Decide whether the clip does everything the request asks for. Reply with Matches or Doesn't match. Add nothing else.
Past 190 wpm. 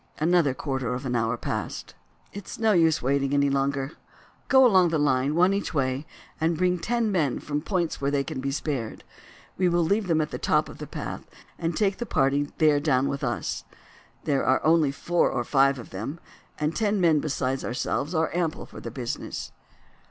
Matches